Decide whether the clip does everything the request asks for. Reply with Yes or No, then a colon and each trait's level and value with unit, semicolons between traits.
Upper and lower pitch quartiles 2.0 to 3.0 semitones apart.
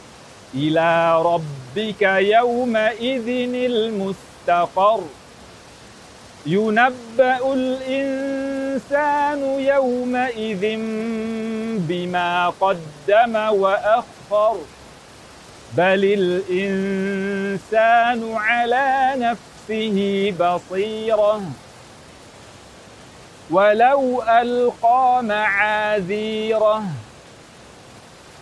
No: average, 4.3 semitones